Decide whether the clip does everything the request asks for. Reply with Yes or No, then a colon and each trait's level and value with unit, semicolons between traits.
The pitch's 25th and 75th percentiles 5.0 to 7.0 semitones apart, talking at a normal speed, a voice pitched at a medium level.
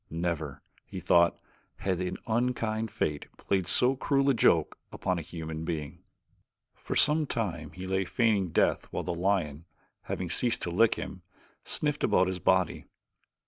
No: average, 5.3 semitones; average, 155 wpm; very low, 95 Hz